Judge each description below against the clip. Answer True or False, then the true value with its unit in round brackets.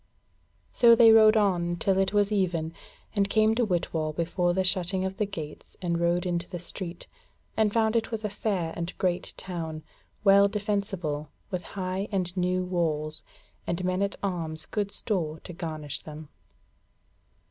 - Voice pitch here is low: False (185 Hz)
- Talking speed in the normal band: True (160 wpm)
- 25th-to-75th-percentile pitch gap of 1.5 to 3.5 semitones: True (3.0 semitones)